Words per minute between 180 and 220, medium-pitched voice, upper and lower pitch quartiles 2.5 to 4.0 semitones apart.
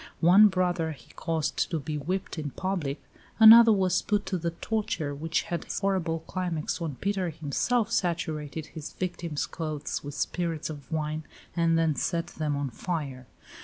No: average, 165 wpm; medium, 165 Hz; average, 3.3 semitones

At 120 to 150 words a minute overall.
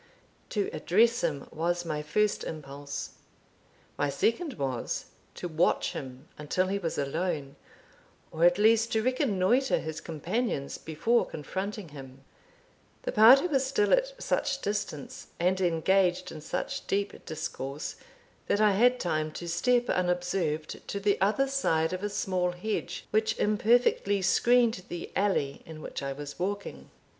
Yes: average, 145 wpm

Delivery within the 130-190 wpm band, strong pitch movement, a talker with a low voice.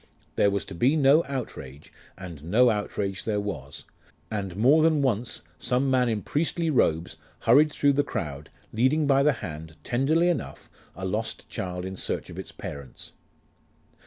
Yes: average, 160 wpm; wide, 7.2 semitones; low, 110 Hz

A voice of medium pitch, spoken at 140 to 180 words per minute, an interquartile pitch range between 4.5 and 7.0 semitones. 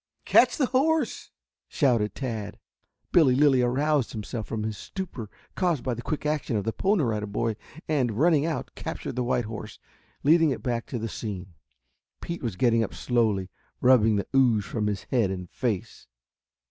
No: low, 120 Hz; average, 170 wpm; wide, 5.4 semitones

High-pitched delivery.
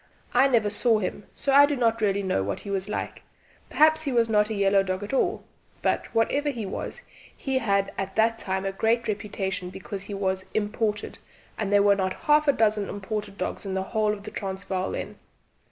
Yes: high, 205 Hz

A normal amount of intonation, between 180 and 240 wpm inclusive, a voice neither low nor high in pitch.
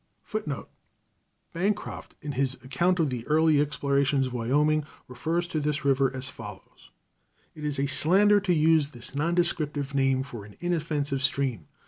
No: average, 3.3 semitones; average, 160 wpm; medium, 145 Hz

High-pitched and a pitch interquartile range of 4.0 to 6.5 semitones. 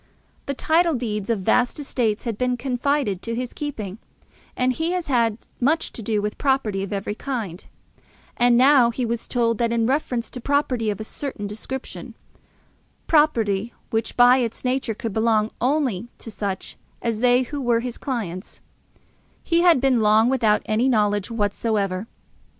No: high, 235 Hz; average, 3.6 semitones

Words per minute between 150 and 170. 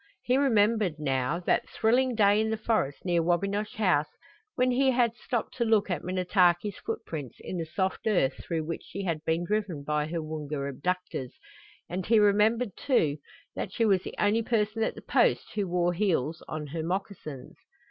No: average, 180 wpm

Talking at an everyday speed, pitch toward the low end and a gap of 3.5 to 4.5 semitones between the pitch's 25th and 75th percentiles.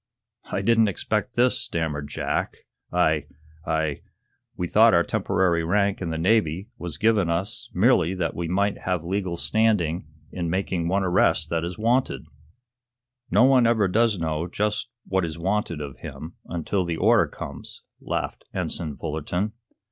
Yes: average, 155 wpm; very low, 90 Hz; average, 4.2 semitones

